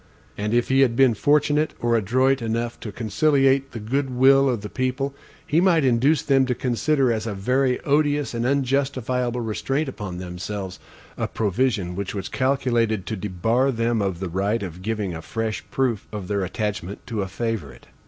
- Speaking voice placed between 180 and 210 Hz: No, low, 120 Hz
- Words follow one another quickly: No, average, 180 wpm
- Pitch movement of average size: Yes, average, 4.5 semitones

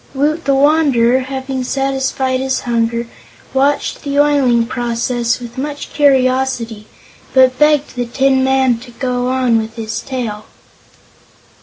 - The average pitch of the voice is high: Yes, very high, 260 Hz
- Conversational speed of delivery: No, slow, 130 wpm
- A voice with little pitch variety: Yes, narrow, 2.2 semitones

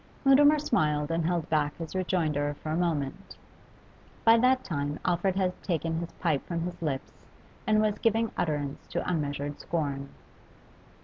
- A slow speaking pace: No, average, 150 wpm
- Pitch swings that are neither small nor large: Yes, average, 4.3 semitones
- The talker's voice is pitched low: No, medium, 165 Hz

